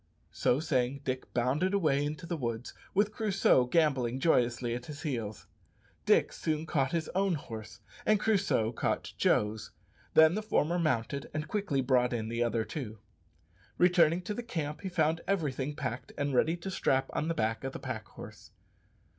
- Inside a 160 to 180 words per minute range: Yes, average, 170 wpm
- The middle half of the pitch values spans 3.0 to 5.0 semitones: No, wide, 5.6 semitones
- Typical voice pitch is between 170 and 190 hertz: No, medium, 145 Hz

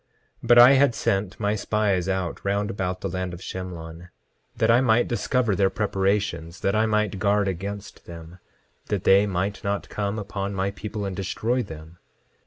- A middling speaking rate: Yes, average, 180 wpm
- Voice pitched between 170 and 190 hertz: No, low, 100 Hz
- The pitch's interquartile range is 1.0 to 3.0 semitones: Yes, narrow, 2.4 semitones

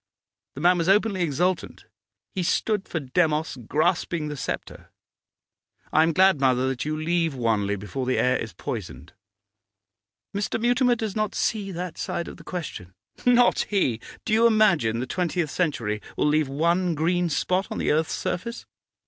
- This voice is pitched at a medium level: Yes, medium, 170 Hz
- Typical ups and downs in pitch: No, wide, 5.7 semitones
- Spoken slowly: No, average, 165 wpm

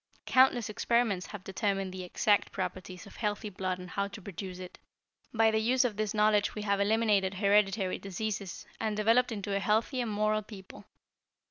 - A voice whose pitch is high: Yes, high, 205 Hz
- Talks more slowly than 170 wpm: No, average, 175 wpm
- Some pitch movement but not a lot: No, narrow, 2.2 semitones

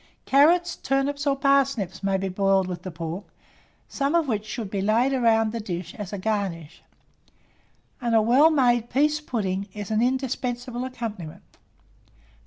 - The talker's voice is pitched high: Yes, high, 230 Hz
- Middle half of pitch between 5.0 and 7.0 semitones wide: Yes, wide, 5.6 semitones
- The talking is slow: No, average, 155 wpm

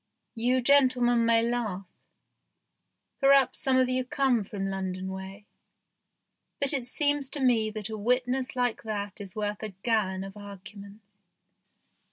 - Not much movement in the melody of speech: No, average, 4.0 semitones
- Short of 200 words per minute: Yes, average, 140 wpm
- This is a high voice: Yes, high, 225 Hz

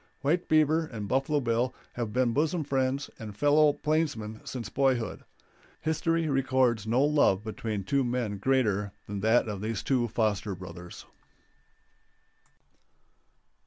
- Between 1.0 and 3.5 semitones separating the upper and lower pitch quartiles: No, average, 5.1 semitones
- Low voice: Yes, low, 125 Hz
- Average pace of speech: No, slow, 125 wpm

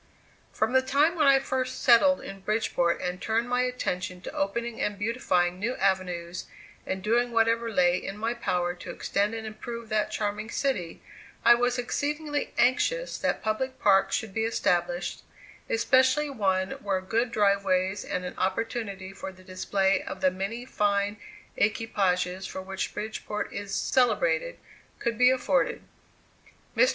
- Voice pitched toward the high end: Yes, high, 215 Hz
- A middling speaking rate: Yes, average, 155 wpm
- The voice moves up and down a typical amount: Yes, average, 4.5 semitones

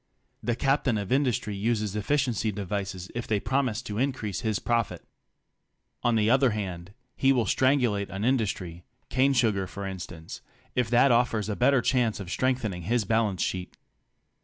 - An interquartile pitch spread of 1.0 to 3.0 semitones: No, average, 4.0 semitones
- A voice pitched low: Yes, low, 110 Hz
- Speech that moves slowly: No, average, 160 wpm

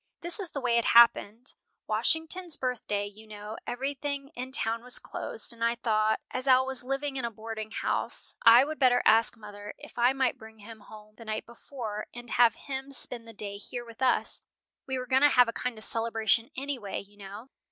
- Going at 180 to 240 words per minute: Yes, fast, 205 wpm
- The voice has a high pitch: Yes, high, 235 Hz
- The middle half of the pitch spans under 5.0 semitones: Yes, average, 3.3 semitones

